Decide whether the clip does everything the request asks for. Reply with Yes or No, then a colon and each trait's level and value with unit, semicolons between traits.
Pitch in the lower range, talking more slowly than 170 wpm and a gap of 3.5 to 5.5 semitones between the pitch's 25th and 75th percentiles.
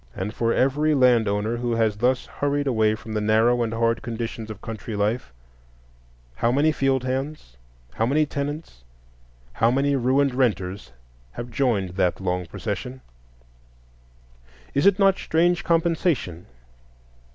Yes: low, 120 Hz; average, 140 wpm; average, 4.5 semitones